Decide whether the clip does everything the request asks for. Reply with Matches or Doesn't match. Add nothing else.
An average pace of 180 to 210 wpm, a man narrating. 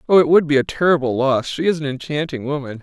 Doesn't match